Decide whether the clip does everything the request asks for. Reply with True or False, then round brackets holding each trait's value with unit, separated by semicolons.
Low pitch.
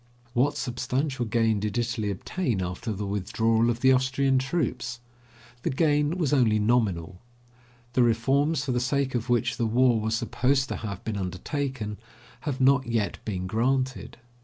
True (120 Hz)